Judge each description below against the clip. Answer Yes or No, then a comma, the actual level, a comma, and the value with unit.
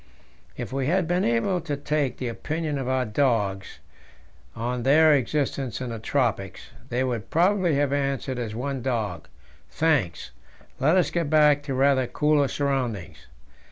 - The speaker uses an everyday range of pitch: Yes, average, 3.8 semitones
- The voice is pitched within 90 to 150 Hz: Yes, low, 135 Hz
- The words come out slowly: No, average, 155 wpm